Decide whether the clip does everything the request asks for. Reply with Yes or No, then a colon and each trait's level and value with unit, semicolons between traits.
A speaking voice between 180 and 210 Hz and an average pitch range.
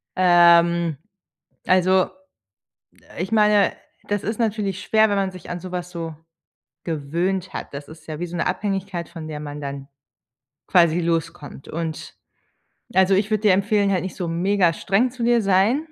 Yes: medium, 185 Hz; average, 3.1 semitones